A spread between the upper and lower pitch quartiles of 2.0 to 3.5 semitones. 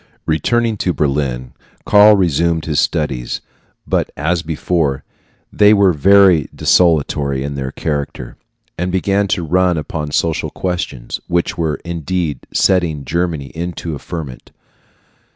No: average, 3.9 semitones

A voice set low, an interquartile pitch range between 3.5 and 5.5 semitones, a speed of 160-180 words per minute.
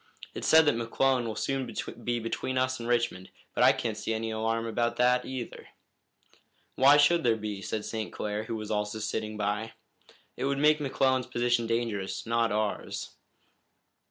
No: low, 115 Hz; average, 2.9 semitones; average, 170 wpm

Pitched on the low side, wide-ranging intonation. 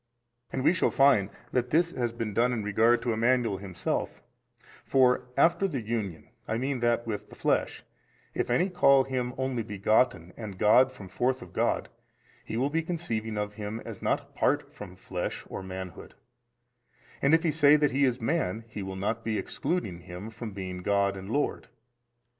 No: low, 115 Hz; average, 4.5 semitones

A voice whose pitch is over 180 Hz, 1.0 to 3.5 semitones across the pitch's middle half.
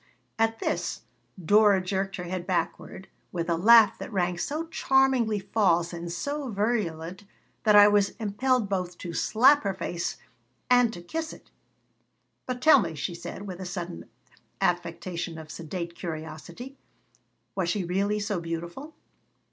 No: high, 190 Hz; average, 4.6 semitones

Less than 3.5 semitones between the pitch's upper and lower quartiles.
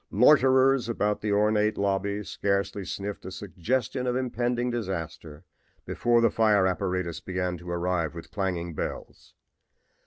No: average, 4.4 semitones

